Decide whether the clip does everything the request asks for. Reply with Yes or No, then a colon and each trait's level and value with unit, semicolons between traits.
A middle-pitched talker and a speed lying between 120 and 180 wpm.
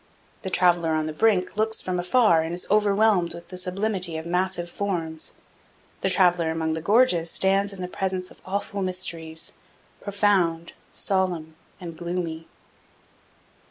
Yes: medium, 180 Hz; average, 145 wpm